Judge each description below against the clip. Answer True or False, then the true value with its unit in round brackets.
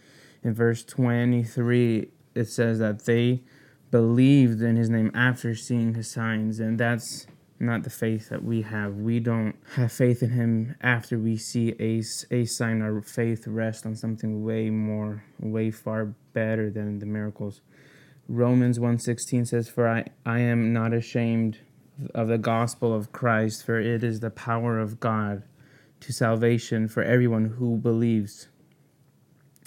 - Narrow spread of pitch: True (1.6 semitones)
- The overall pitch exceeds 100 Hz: True (115 Hz)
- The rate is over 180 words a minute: False (150 wpm)